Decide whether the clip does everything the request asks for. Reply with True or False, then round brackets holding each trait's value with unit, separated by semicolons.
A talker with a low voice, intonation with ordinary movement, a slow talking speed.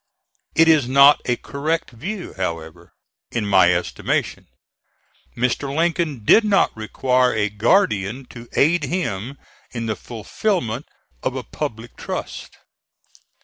False (125 Hz; 6.4 semitones; 120 wpm)